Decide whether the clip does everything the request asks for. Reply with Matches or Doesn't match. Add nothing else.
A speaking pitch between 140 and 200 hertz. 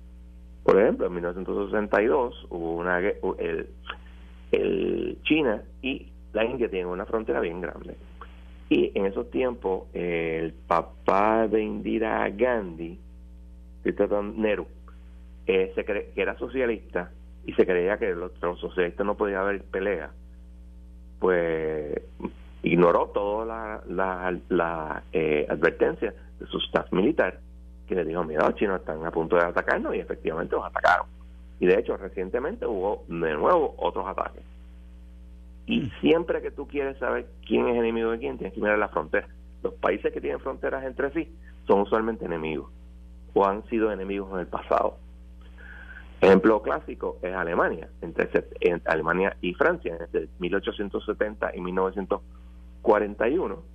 Doesn't match